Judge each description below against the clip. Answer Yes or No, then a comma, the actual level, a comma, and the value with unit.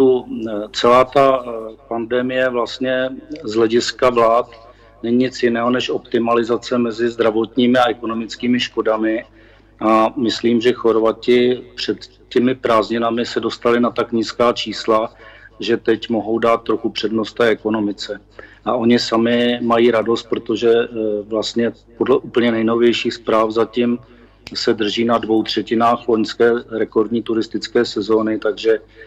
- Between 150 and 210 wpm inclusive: No, average, 125 wpm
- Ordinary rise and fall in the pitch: No, narrow, 1.4 semitones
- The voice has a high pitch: No, low, 115 Hz